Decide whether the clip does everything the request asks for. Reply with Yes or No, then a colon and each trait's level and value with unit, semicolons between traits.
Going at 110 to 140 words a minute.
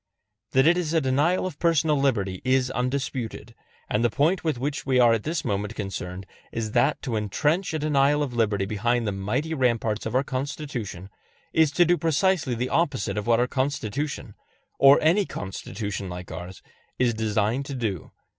No: average, 180 wpm